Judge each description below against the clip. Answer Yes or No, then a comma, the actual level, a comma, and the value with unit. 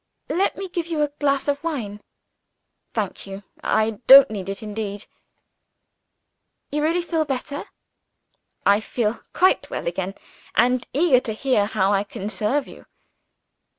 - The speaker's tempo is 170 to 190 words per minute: No, average, 145 wpm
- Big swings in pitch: Yes, wide, 6.3 semitones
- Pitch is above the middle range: Yes, high, 245 Hz